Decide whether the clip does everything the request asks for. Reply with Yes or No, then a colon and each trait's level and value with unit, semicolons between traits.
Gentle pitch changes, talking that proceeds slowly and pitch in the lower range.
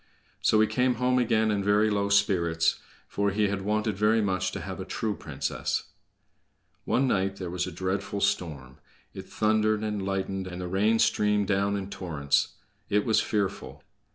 No: narrow, 2.3 semitones; average, 175 wpm; low, 100 Hz